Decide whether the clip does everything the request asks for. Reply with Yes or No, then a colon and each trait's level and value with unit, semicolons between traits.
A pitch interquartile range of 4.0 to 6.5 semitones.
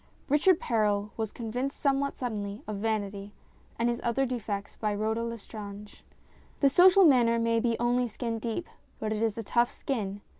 No: average, 2.8 semitones